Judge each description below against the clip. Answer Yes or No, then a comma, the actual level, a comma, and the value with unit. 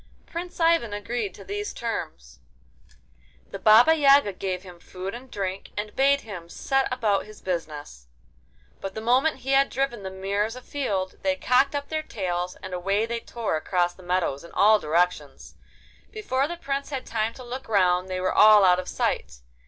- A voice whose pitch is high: Yes, high, 215 Hz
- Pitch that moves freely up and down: Yes, wide, 6.5 semitones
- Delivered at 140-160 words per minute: No, average, 180 wpm